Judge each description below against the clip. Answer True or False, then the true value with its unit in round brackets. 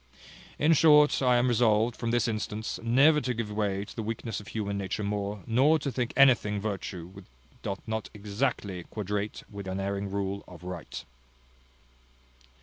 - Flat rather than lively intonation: False (3.4 semitones)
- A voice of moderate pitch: False (105 Hz)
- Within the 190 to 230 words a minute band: False (165 wpm)